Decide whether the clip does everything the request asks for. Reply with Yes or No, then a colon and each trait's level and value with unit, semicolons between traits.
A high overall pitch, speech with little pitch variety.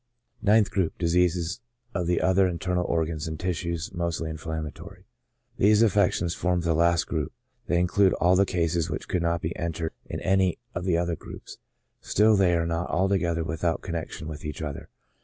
No: very low, 85 Hz; narrow, 1.9 semitones